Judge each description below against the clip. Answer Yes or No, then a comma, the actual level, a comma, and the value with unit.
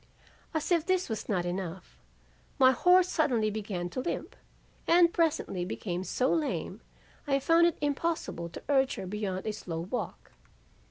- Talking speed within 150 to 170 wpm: Yes, average, 155 wpm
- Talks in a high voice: Yes, very high, 250 Hz